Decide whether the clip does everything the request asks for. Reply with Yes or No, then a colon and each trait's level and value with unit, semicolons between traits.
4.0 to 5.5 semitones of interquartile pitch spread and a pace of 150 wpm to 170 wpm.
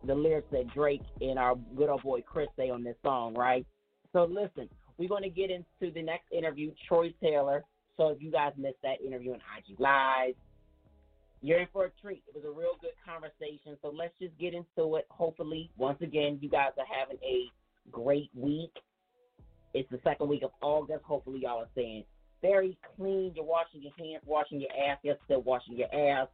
No: average, 4.3 semitones; average, 200 wpm